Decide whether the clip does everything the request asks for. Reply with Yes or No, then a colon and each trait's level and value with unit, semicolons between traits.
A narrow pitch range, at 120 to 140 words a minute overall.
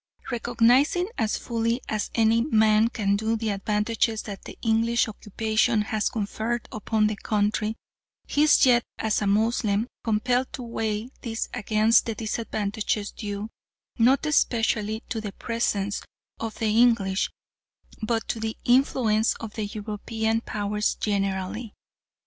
Yes: narrow, 1.7 semitones; slow, 135 wpm